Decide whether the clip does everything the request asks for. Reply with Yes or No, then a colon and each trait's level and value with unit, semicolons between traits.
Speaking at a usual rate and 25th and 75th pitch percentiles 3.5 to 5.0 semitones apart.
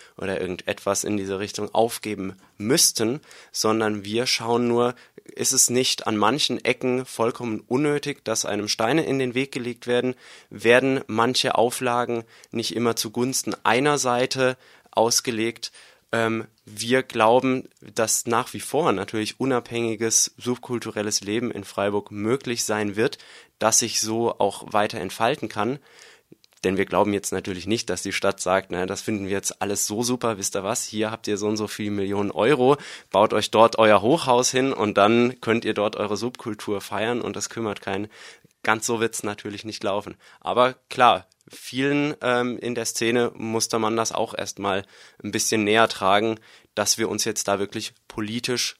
No: average, 170 wpm; average, 2.7 semitones